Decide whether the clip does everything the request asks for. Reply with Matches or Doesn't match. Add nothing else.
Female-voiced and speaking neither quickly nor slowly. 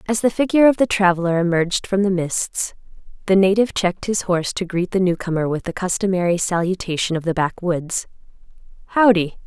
Matches